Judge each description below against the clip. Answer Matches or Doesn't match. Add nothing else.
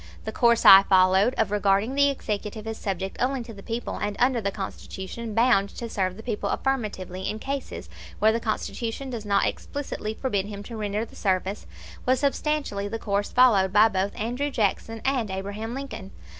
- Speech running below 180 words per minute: Doesn't match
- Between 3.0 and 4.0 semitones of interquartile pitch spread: Matches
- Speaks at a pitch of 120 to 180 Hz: Doesn't match